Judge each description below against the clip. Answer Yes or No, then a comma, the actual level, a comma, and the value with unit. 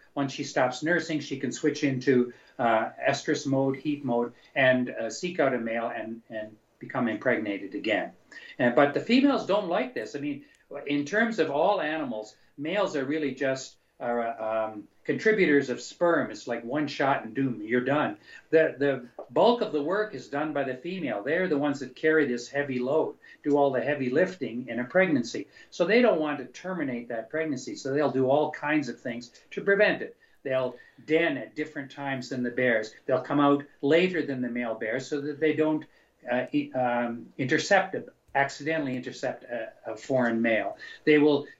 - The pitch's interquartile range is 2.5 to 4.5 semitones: Yes, average, 3.6 semitones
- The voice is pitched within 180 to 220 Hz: No, medium, 140 Hz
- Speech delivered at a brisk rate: No, average, 190 wpm